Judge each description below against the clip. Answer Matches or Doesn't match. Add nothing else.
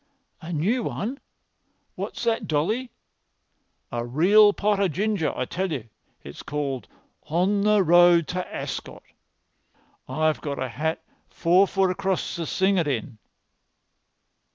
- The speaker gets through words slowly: Matches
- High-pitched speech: Doesn't match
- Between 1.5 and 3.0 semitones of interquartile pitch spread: Doesn't match